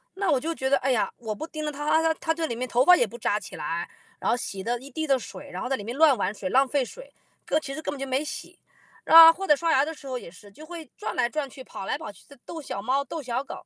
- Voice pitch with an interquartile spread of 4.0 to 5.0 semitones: Yes, average, 4.3 semitones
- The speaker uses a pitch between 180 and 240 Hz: No, very high, 275 Hz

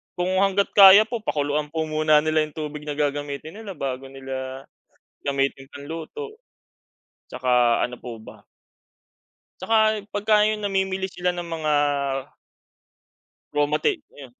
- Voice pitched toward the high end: No, medium, 155 Hz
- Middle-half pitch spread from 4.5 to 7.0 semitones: Yes, wide, 5.6 semitones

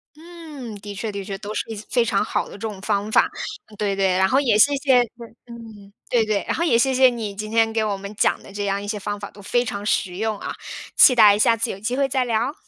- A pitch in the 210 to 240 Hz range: Yes, high, 215 Hz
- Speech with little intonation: No, average, 3.2 semitones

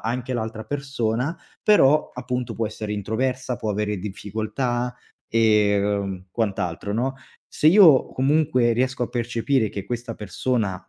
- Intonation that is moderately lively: Yes, average, 3.5 semitones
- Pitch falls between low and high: No, low, 120 Hz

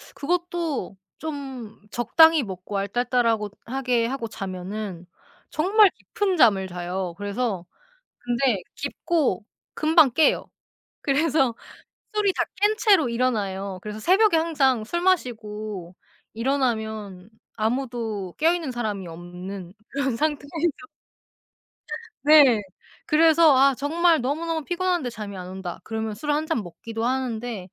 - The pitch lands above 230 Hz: Yes, high, 245 Hz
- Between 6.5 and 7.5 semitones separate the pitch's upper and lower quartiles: Yes, wide, 6.9 semitones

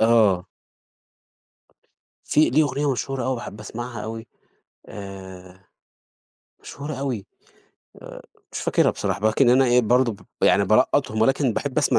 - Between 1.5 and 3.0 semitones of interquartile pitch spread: No, average, 4.1 semitones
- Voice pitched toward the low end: Yes, low, 120 Hz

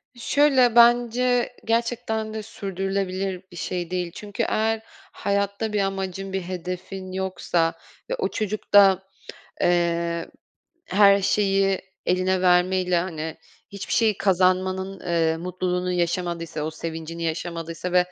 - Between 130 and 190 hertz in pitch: Yes, medium, 185 Hz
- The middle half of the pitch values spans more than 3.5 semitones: No, narrow, 2.5 semitones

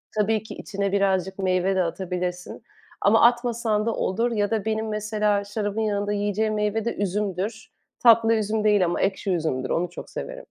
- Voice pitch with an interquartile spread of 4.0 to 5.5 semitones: No, narrow, 2.4 semitones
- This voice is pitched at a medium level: No, high, 205 Hz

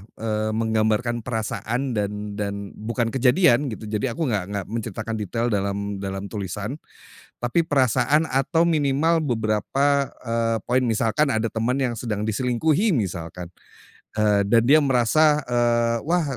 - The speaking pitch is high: No, low, 115 Hz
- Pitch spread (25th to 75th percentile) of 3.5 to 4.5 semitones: Yes, average, 4.1 semitones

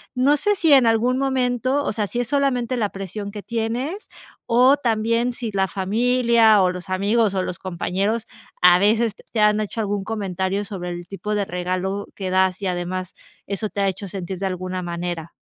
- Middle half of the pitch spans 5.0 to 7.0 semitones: No, average, 4.0 semitones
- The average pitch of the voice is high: Yes, high, 205 Hz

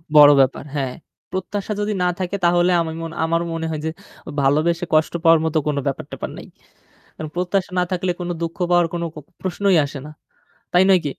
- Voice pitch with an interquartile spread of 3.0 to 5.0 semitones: No, narrow, 2.6 semitones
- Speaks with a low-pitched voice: No, medium, 170 Hz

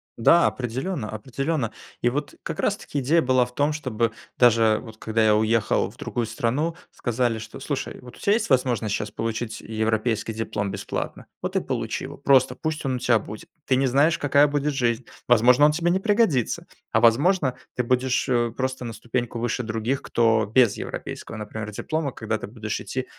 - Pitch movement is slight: No, average, 3.6 semitones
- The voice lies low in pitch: Yes, low, 120 Hz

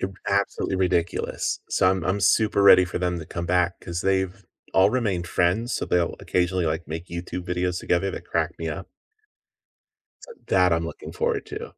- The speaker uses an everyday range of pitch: No, narrow, 1.7 semitones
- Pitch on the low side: Yes, very low, 90 Hz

